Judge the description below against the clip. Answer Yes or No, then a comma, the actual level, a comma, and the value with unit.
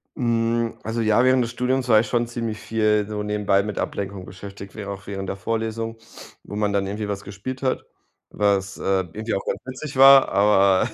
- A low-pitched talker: Yes, low, 110 Hz